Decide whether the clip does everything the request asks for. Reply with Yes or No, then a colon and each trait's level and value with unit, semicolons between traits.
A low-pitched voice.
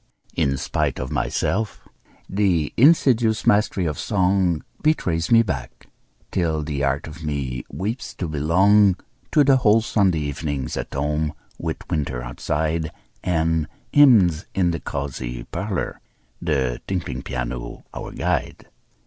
Yes: very low, 80 Hz